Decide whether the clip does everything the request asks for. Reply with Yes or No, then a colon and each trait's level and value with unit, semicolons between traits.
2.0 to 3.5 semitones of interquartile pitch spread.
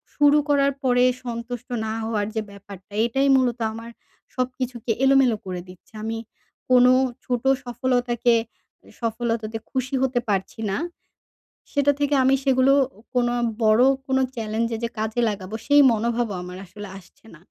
Yes: average, 3.0 semitones